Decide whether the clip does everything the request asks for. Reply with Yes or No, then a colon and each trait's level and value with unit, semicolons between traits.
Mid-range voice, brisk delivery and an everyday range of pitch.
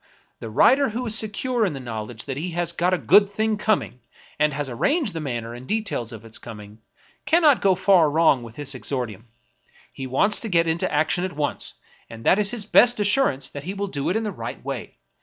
No: medium, 170 Hz; fast, 225 wpm; wide, 8.4 semitones